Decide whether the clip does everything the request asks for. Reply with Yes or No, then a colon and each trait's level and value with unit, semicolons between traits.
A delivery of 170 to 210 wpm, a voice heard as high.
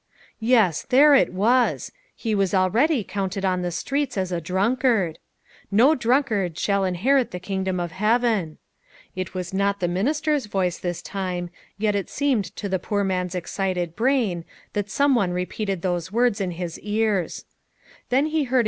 No: average, 155 wpm; high, 195 Hz